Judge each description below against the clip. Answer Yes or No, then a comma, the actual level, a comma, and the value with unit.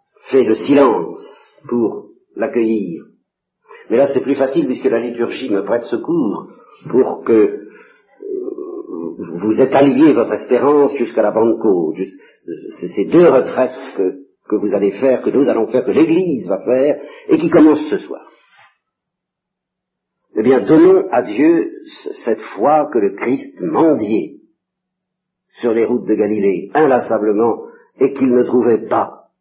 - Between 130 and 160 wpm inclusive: Yes, slow, 145 wpm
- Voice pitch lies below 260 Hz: No, very high, 330 Hz